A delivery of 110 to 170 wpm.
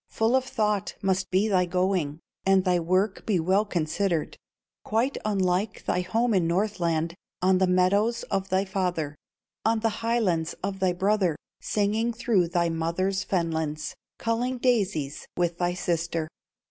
Yes: average, 145 wpm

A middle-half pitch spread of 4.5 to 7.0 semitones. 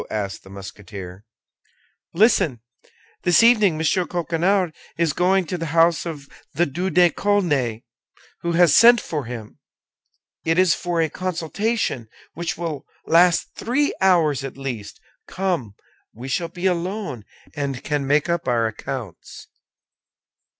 Yes: average, 5.2 semitones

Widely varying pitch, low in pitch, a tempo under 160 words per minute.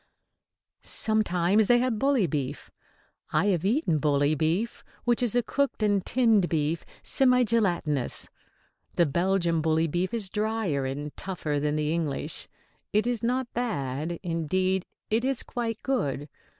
No: wide, 6.8 semitones; medium, 185 Hz; average, 145 wpm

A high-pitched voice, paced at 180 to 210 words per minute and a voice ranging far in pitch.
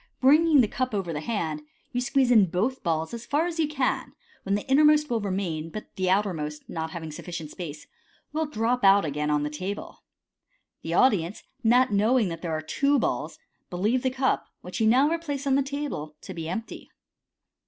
Yes: high, 210 Hz; average, 195 wpm; wide, 8.1 semitones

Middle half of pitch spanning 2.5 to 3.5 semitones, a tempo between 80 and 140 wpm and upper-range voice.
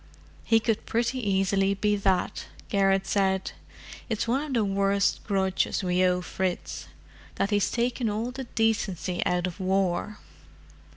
Yes: average, 2.8 semitones; slow, 135 wpm; high, 200 Hz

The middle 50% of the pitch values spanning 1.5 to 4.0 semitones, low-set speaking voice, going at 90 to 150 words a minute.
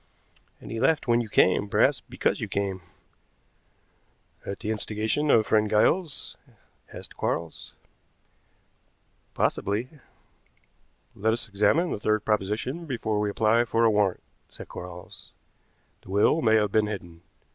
Yes: narrow, 2.5 semitones; low, 110 Hz; slow, 135 wpm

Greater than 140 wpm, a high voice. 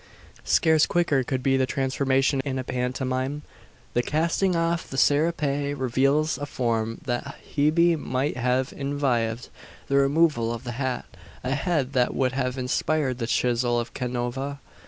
No: average, 150 wpm; low, 135 Hz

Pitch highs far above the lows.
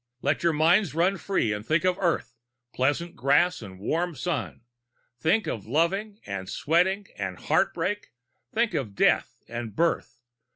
Yes: wide, 7.1 semitones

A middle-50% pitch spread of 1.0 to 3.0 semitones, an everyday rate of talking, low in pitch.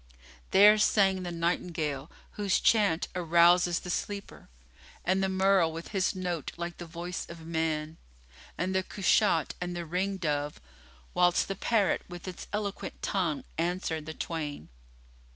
No: narrow, 2.6 semitones; average, 145 wpm; medium, 175 Hz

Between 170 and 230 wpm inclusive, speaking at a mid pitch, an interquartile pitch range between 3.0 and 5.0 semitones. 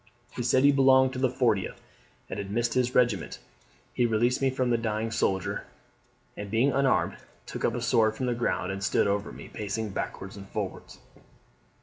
No: average, 190 wpm; low, 115 Hz; average, 3.8 semitones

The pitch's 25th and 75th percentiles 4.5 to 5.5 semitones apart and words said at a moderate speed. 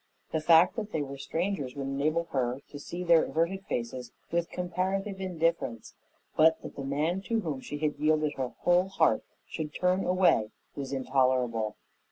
Yes: average, 4.8 semitones; average, 170 wpm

